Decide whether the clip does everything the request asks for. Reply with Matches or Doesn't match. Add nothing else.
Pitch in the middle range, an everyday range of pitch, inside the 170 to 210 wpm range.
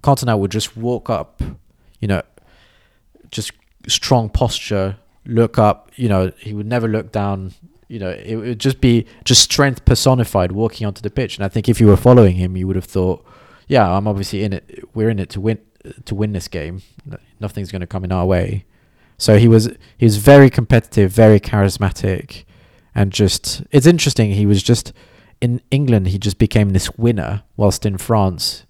Doesn't match